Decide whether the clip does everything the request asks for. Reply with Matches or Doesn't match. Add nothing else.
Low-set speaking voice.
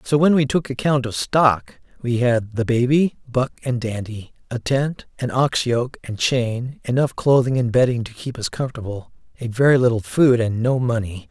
Matches